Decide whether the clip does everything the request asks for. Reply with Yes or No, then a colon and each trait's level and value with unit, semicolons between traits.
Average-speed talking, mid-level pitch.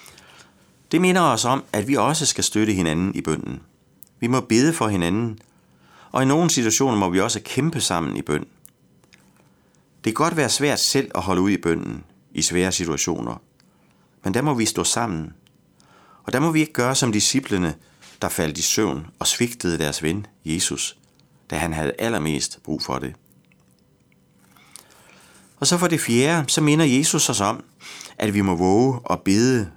No: average, 175 wpm; low, 110 Hz